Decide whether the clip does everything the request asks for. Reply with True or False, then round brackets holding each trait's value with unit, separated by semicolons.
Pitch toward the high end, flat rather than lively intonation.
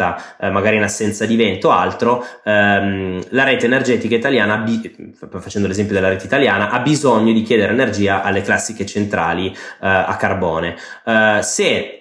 False (105 Hz; 2.3 semitones)